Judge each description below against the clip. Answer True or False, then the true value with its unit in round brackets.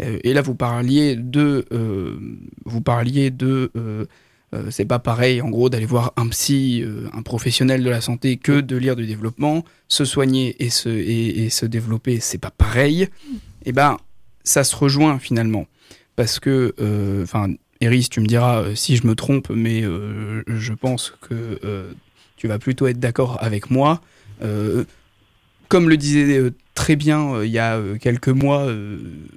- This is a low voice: True (120 Hz)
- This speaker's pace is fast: False (180 wpm)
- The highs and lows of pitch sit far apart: False (3.3 semitones)